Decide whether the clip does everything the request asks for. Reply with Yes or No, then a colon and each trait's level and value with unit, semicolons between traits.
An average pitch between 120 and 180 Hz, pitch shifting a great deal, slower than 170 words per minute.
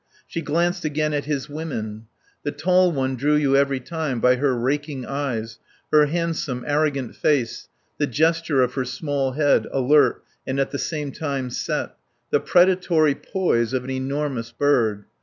No: medium, 140 Hz; average, 3.0 semitones; average, 160 wpm